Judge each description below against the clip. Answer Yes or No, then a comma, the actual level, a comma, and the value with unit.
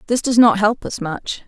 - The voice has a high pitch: Yes, high, 220 Hz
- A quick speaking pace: Yes, fast, 245 wpm